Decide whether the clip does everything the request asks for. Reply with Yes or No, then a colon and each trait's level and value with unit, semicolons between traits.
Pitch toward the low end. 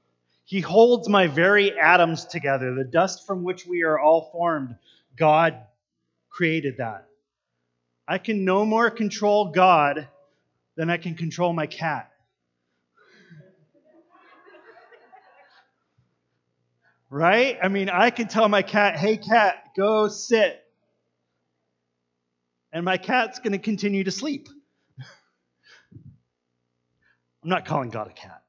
No: medium, 165 Hz